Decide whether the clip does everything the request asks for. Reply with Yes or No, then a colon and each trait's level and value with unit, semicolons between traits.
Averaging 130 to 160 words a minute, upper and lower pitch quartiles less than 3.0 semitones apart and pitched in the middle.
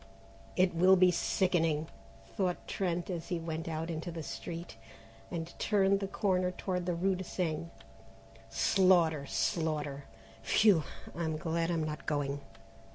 Yes: average, 140 wpm; narrow, 2.5 semitones; medium, 170 Hz